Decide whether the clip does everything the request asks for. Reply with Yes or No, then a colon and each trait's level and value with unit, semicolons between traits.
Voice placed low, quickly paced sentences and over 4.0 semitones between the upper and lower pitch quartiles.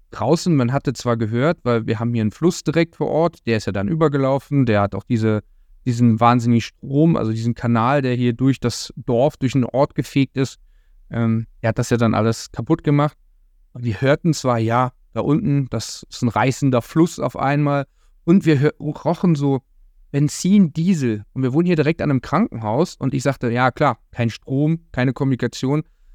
Yes: low, 130 Hz; fast, 195 wpm; average, 4.4 semitones